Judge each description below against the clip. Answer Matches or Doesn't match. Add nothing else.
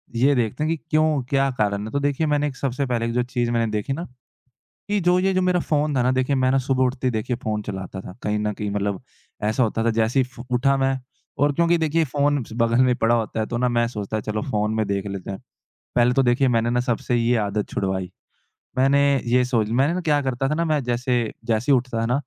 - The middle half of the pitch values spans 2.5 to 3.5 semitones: Doesn't match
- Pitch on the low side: Matches